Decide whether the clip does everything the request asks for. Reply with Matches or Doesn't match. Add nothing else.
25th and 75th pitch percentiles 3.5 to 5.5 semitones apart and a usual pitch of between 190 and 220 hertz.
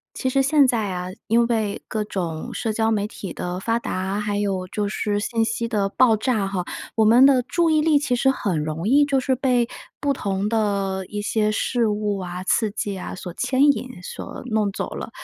Matches